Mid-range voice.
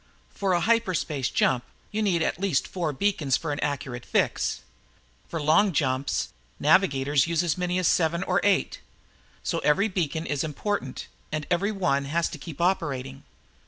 Yes: medium, 165 Hz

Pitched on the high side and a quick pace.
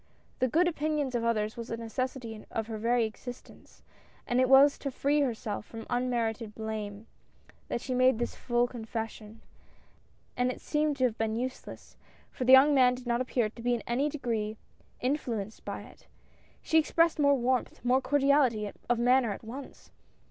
No: high, 245 Hz; average, 185 wpm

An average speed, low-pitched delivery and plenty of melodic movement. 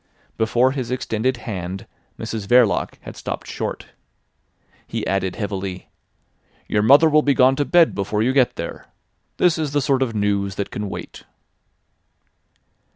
No: average, 150 wpm; low, 115 Hz; average, 4.9 semitones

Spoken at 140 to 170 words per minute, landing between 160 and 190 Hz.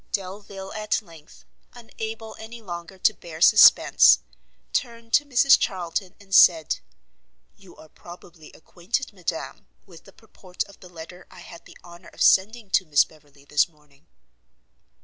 Yes: average, 150 wpm; medium, 185 Hz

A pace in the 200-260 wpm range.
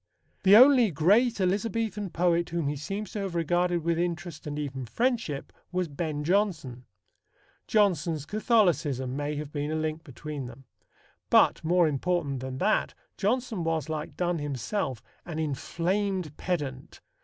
No: average, 145 wpm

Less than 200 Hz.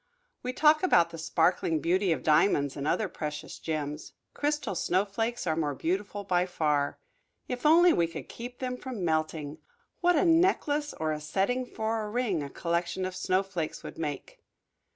Yes: medium, 185 Hz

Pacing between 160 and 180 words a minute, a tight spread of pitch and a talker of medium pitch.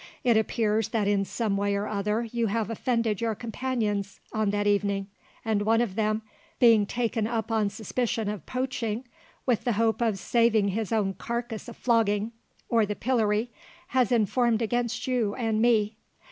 No: average, 170 wpm; narrow, 2.2 semitones; high, 220 Hz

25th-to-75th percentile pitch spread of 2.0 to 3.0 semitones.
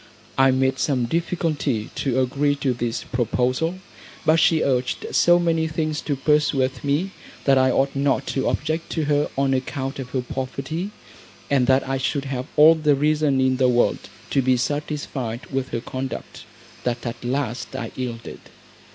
Yes: narrow, 2.6 semitones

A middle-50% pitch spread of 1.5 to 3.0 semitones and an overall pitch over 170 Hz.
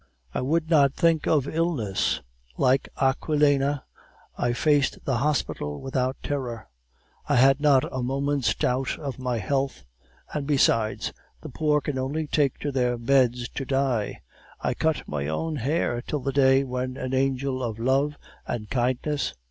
No: narrow, 2.5 semitones; low, 135 Hz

